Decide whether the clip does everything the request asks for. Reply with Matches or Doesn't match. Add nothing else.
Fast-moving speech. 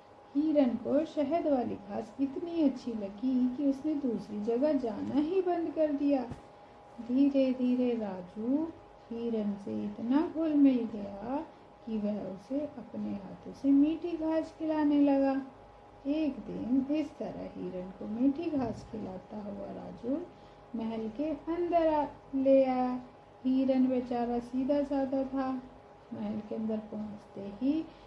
Doesn't match